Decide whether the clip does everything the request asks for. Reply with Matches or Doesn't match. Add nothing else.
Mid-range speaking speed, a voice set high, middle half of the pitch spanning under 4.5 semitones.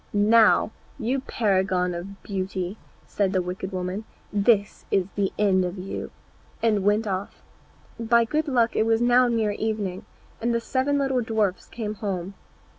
Matches